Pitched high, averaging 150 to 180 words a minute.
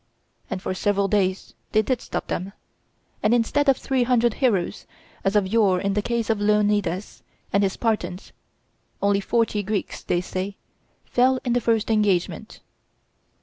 Yes: high, 210 Hz; average, 155 wpm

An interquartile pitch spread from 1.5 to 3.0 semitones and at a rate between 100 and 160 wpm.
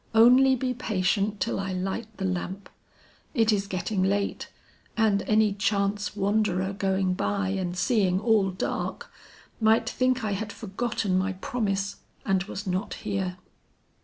Yes: narrow, 2.4 semitones; average, 140 wpm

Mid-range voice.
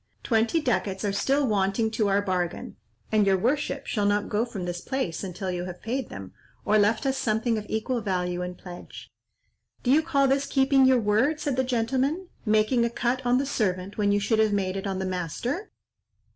No: high, 220 Hz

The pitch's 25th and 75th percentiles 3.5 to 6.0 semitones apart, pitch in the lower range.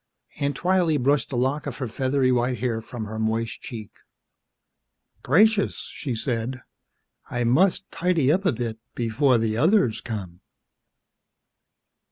Yes: average, 4.5 semitones; low, 125 Hz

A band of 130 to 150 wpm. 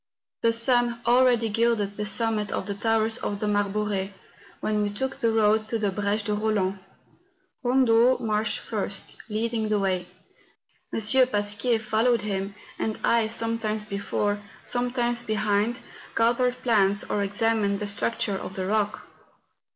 Yes: average, 145 wpm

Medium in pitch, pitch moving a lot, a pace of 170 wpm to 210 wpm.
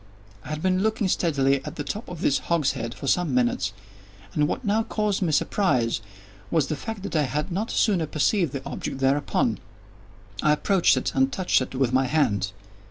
Yes: medium, 150 Hz; wide, 5.9 semitones; average, 190 wpm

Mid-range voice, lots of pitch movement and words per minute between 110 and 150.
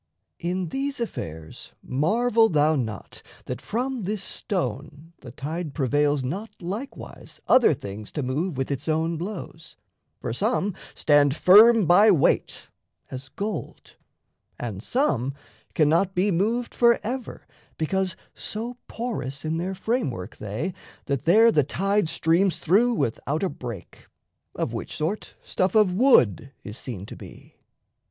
Yes: medium, 170 Hz; wide, 7.3 semitones; slow, 135 wpm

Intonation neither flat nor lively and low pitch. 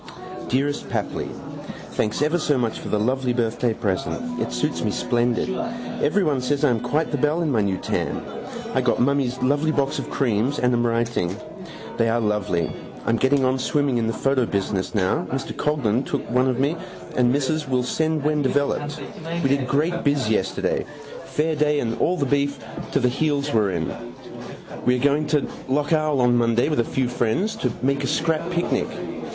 Yes: average, 3.9 semitones; low, 130 Hz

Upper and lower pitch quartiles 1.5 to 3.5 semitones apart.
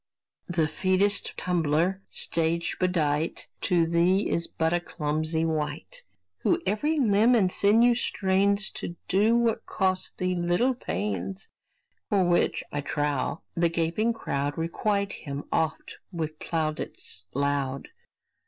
No: average, 4.5 semitones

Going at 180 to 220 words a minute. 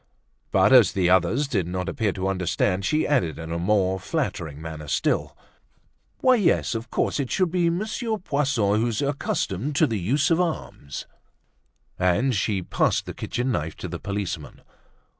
No: average, 165 wpm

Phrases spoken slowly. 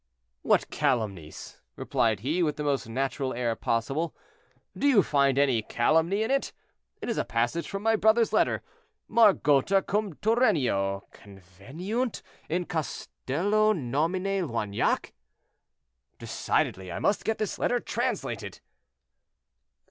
Yes: slow, 115 wpm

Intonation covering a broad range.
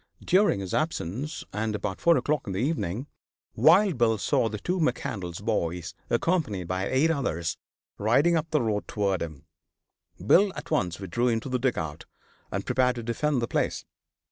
Yes: wide, 7.9 semitones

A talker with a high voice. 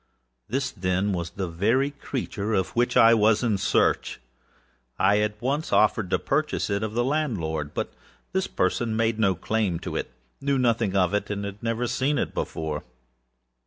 No: low, 110 Hz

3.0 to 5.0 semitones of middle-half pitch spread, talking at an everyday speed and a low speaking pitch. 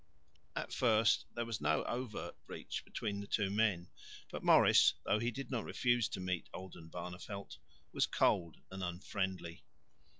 Yes: average, 4.1 semitones; average, 145 wpm; low, 100 Hz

